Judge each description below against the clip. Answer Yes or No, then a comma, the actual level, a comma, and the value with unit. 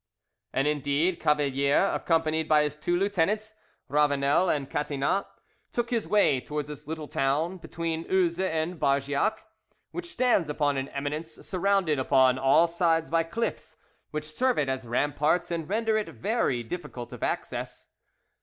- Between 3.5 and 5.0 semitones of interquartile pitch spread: Yes, average, 4.2 semitones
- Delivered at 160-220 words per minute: No, average, 145 wpm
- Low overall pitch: No, medium, 155 Hz